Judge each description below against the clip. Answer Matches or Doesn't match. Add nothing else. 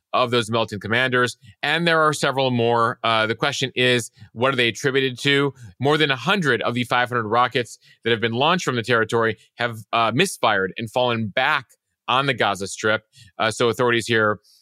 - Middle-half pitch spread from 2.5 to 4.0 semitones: Matches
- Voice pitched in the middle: Doesn't match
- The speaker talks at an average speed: Matches